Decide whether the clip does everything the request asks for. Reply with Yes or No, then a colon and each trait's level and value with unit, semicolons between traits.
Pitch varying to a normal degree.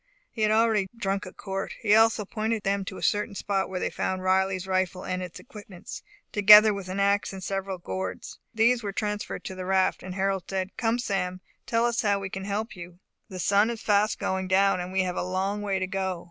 No: narrow, 1.9 semitones